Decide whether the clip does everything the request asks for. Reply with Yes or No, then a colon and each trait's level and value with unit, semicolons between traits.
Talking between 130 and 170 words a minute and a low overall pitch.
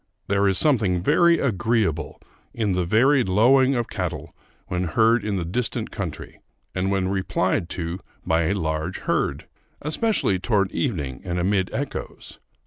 Yes: average, 145 wpm; very low, 95 Hz